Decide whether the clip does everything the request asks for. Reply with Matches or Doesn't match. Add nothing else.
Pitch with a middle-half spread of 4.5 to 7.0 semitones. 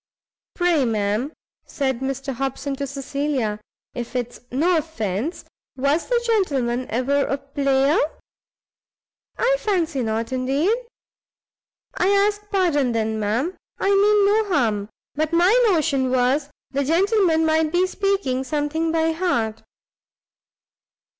Matches